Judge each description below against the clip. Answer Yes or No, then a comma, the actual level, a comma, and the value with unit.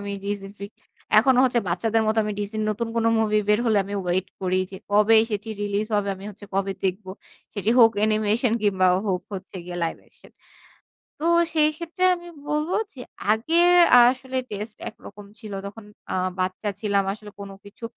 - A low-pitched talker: No, high, 210 Hz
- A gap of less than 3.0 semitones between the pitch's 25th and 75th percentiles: Yes, narrow, 2.4 semitones